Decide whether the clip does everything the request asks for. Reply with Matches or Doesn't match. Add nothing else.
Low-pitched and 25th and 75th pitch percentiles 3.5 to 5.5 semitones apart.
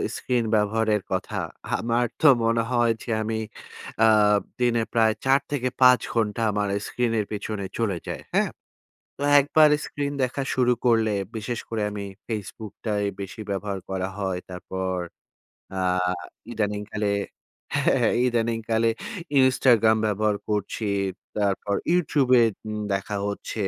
Doesn't match